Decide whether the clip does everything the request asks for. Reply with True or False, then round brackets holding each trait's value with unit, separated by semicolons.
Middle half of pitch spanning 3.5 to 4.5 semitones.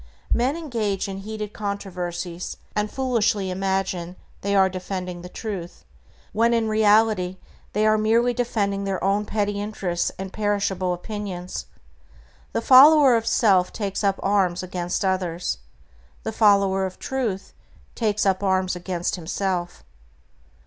False (2.7 semitones)